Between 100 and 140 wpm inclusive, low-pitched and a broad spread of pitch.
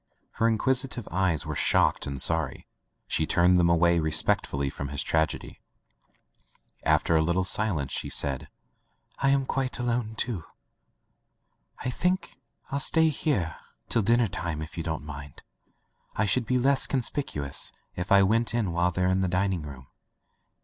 No: average, 155 wpm; very low, 90 Hz; wide, 7.0 semitones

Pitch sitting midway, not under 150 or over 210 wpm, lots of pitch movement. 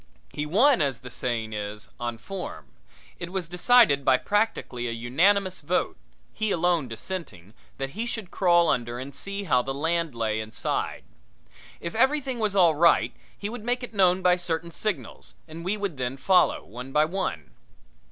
Yes: medium, 170 Hz; average, 170 wpm; wide, 7.7 semitones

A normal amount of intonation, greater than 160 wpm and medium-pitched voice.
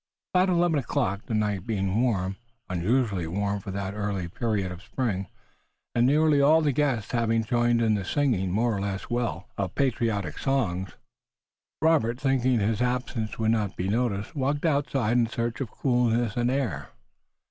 No: average, 4.4 semitones; average, 170 wpm; low, 115 Hz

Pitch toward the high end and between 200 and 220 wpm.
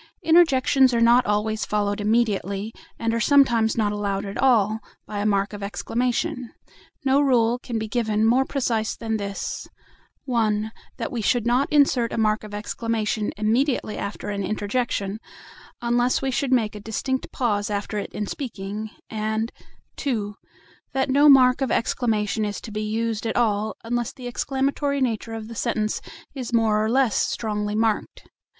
No: high, 225 Hz; average, 165 wpm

